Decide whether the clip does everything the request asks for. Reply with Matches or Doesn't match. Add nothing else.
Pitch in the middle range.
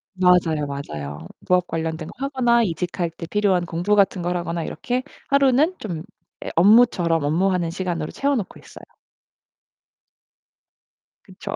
Matches